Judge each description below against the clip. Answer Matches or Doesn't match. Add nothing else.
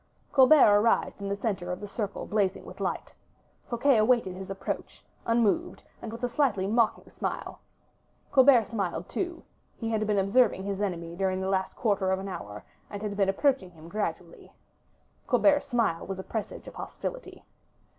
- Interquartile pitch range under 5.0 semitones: Matches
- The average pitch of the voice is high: Matches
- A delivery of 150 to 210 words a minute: Matches